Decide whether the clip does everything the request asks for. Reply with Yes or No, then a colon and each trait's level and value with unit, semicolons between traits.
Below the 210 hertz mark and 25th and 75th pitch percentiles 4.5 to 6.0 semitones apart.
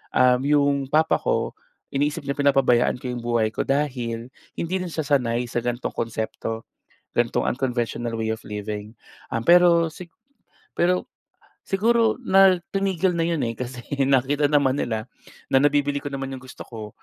Yes: low, 135 Hz; average, 5.0 semitones